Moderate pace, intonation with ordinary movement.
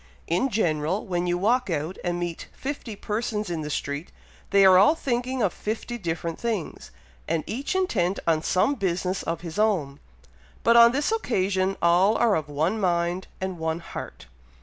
Yes: average, 170 wpm; average, 4.7 semitones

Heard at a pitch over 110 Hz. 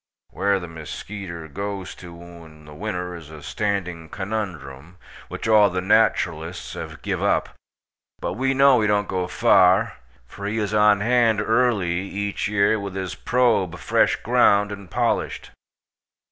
No: low, 100 Hz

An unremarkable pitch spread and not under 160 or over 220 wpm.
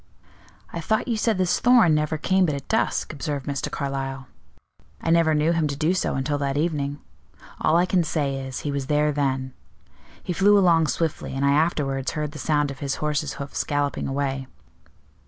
Yes: average, 3.1 semitones; average, 190 wpm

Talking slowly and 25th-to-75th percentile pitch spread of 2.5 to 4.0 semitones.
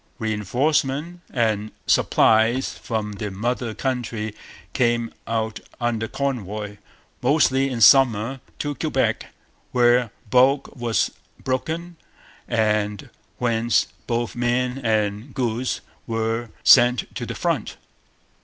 Yes: slow, 100 wpm; average, 2.9 semitones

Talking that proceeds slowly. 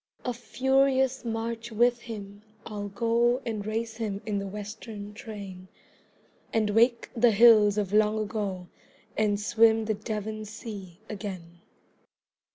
Yes: slow, 130 wpm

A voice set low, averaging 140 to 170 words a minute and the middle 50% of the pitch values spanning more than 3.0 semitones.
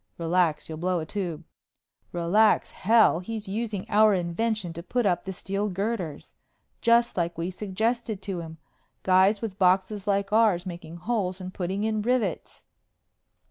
No: high, 190 Hz; average, 150 wpm; average, 3.7 semitones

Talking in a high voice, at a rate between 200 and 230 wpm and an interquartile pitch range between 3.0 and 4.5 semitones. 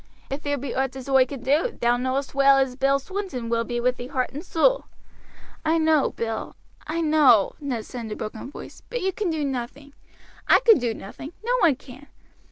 Yes: very high, 275 Hz; fast, 205 wpm; average, 3.9 semitones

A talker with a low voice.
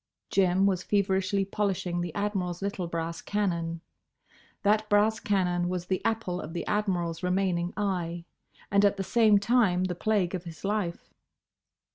No: high, 190 Hz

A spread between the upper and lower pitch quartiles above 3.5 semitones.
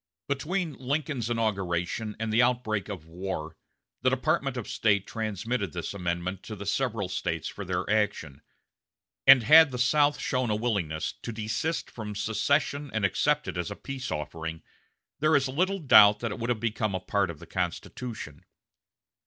Yes: wide, 5.4 semitones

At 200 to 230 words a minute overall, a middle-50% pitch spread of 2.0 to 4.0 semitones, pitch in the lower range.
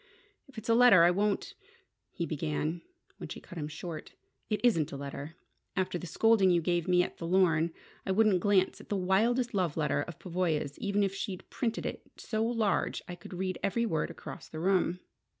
No: fast, 205 wpm; average, 3.6 semitones; medium, 185 Hz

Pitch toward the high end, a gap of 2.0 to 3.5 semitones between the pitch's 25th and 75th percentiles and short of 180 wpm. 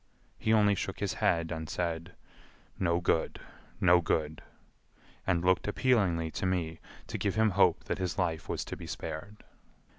No: very low, 90 Hz; average, 3.1 semitones; average, 160 wpm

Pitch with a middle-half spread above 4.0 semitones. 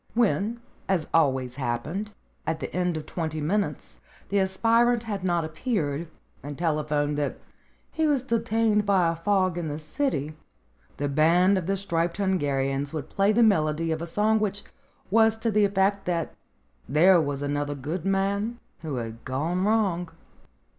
Yes: average, 5.2 semitones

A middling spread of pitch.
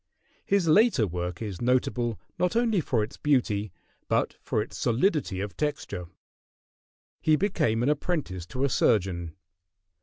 No: wide, 7.6 semitones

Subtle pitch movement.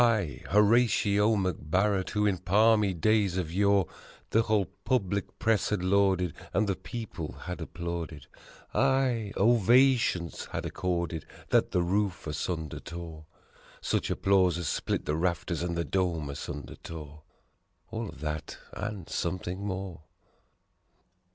No: average, 3.6 semitones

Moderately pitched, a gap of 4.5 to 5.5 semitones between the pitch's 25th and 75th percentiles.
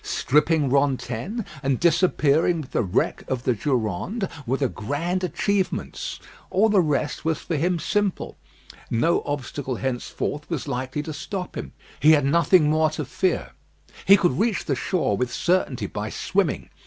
Yes: medium, 150 Hz; average, 5.1 semitones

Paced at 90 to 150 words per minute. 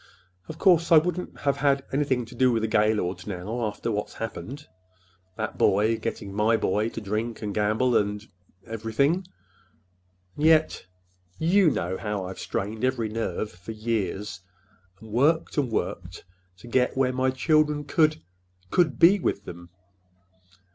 Yes: average, 140 wpm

